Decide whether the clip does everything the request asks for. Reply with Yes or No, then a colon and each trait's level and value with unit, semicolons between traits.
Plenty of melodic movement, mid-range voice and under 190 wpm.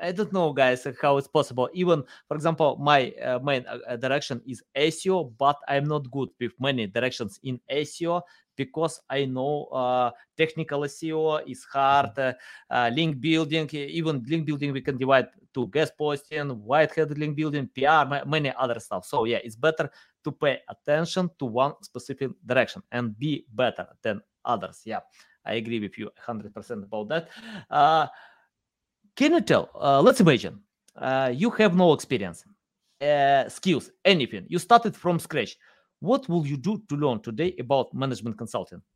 No: average, 3.8 semitones; medium, 145 Hz; average, 170 wpm